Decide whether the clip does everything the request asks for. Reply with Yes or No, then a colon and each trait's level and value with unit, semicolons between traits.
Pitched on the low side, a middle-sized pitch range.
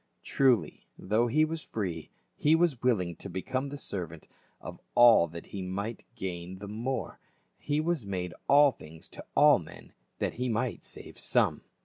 No: low, 110 Hz; wide, 6.5 semitones